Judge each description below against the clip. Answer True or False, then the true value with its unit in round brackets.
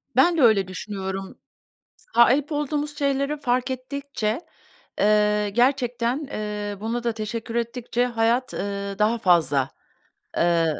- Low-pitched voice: False (235 Hz)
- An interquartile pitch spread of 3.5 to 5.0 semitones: True (3.9 semitones)